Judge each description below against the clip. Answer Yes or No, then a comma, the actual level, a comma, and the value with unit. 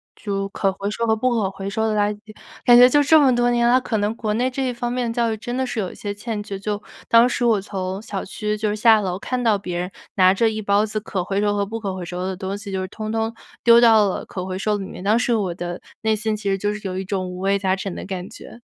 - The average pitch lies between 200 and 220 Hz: Yes, high, 210 Hz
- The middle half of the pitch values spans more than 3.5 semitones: No, average, 2.8 semitones